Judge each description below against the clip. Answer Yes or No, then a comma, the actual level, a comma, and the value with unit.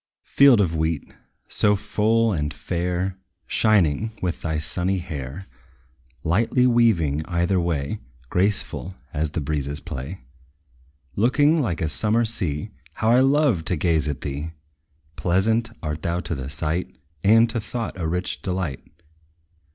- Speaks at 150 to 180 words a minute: No, slow, 135 wpm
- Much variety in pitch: Yes, wide, 5.9 semitones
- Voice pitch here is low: Yes, very low, 90 Hz